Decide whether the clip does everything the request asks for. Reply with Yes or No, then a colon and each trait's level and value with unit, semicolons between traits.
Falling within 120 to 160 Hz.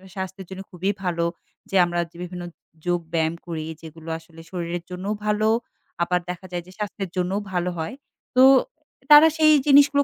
No: medium, 180 Hz